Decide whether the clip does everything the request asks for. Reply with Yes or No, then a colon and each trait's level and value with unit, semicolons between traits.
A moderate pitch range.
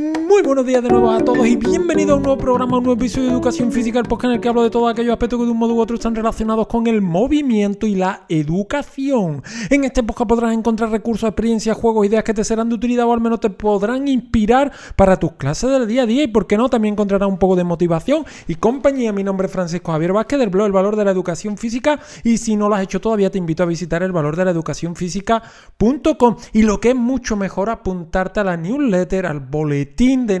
Yes: average, 4.3 semitones